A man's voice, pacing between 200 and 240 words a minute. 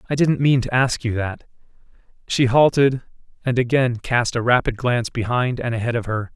No: male; average, 190 wpm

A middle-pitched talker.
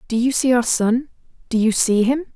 No: high, 240 Hz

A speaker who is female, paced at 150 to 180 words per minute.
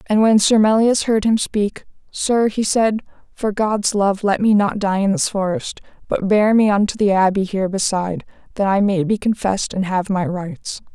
No: female; fast, 205 wpm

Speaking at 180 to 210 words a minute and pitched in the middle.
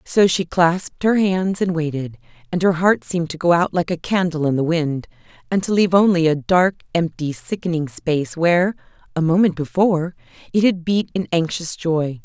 Yes: average, 190 wpm; medium, 170 Hz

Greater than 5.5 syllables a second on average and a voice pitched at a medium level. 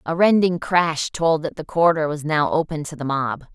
No: 5.0 syllables/s; medium, 155 Hz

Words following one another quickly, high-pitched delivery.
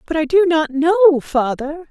No: average, 190 wpm; very high, 315 Hz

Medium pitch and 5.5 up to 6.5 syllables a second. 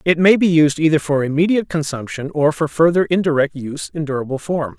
Yes: medium, 155 Hz; 6.0 syllables/s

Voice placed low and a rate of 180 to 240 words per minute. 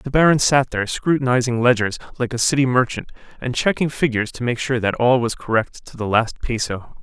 Yes: low, 125 Hz; fast, 205 wpm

